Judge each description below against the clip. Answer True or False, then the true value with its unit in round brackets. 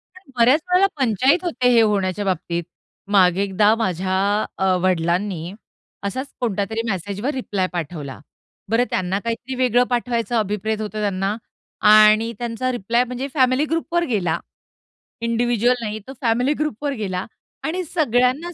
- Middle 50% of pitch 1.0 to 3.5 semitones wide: False (4.6 semitones)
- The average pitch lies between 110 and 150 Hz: False (225 Hz)